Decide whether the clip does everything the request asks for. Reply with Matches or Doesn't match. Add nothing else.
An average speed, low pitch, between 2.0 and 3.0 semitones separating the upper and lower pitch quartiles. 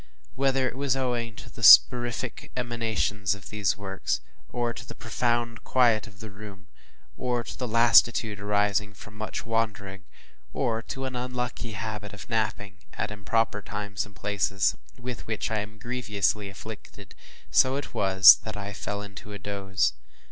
Matches